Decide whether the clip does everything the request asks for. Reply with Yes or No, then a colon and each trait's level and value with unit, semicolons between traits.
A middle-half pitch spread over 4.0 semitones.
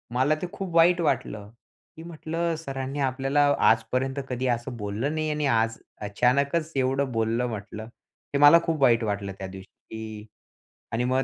Yes: average, 4.6 semitones